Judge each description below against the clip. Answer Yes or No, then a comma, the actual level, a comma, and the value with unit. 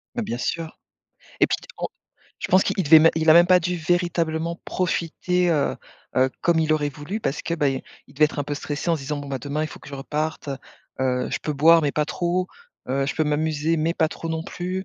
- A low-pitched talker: No, medium, 155 Hz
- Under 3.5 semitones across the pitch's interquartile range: Yes, average, 2.7 semitones